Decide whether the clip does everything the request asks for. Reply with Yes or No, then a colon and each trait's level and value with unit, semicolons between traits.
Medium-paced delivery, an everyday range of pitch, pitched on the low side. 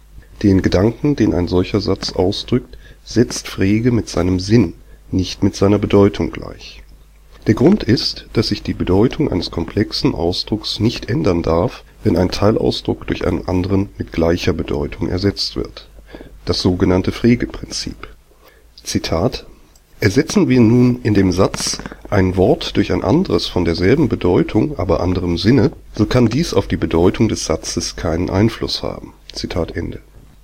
Yes: average, 150 wpm; average, 3.8 semitones; very low, 95 Hz